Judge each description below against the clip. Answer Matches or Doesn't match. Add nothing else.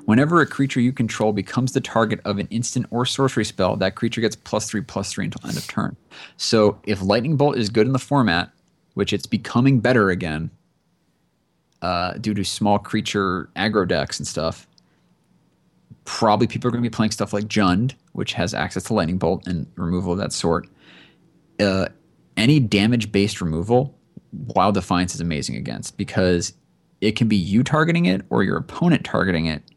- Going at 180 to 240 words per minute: Matches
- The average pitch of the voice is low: Matches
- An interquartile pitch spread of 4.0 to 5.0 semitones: Matches